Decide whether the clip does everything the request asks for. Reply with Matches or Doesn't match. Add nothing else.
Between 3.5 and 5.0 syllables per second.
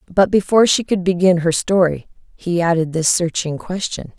Doesn't match